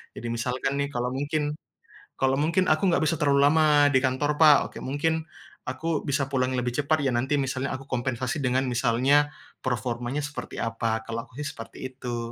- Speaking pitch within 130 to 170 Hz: Yes, low, 135 Hz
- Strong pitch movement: No, average, 2.9 semitones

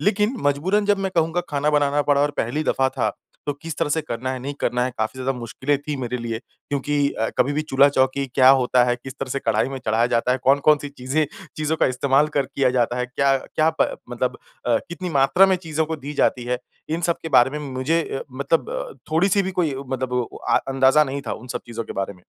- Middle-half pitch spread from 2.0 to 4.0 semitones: Yes, average, 3.2 semitones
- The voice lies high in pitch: No, medium, 140 Hz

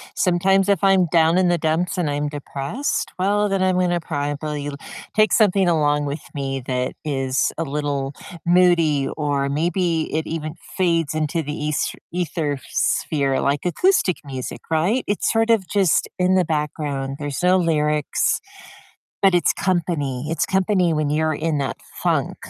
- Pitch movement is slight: No, average, 3.8 semitones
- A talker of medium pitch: Yes, medium, 160 Hz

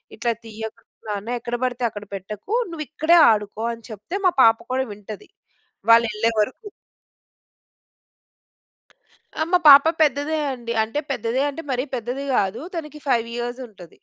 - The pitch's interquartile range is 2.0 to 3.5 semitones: No, average, 4.3 semitones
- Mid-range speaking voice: No, high, 235 Hz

